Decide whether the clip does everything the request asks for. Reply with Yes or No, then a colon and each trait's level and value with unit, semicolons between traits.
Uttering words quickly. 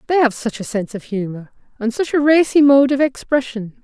Yes: fast, 220 wpm